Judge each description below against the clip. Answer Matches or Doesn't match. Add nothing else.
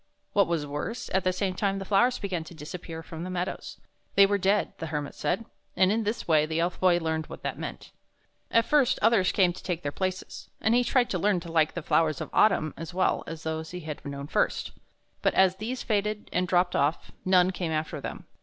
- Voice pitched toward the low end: Doesn't match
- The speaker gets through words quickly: Matches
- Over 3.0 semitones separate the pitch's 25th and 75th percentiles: Matches